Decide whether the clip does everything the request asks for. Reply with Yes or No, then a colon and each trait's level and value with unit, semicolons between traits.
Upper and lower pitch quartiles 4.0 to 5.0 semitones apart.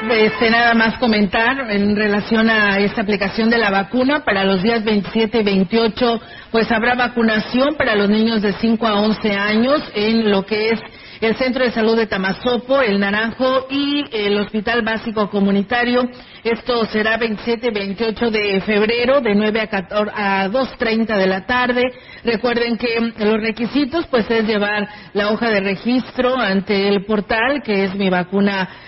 No: narrow, 2.4 semitones